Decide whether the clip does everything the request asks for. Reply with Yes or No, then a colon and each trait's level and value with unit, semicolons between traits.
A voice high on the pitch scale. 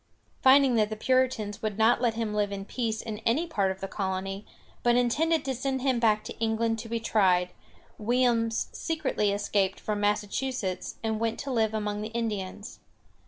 Yes: high, 220 Hz